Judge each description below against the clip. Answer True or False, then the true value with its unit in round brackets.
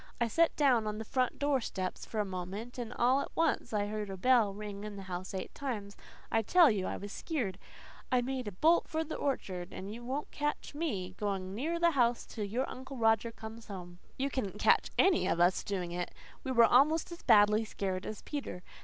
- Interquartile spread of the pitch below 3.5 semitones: False (5.1 semitones)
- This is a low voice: False (225 Hz)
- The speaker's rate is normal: False (220 wpm)